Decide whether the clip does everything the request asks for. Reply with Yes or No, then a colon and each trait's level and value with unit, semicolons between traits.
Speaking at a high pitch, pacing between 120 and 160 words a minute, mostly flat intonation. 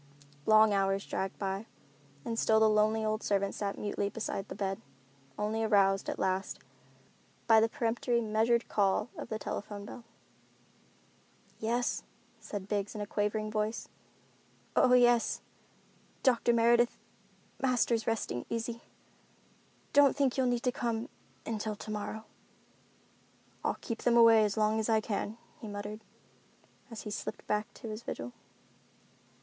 Yes: high, 220 Hz; average, 140 wpm; narrow, 2.0 semitones